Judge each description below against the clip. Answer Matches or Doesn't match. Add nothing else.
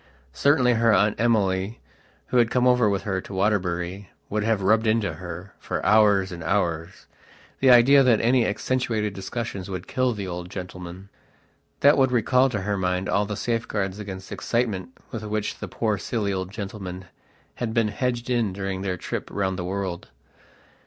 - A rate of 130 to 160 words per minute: Doesn't match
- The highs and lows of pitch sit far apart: Doesn't match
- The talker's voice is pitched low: Matches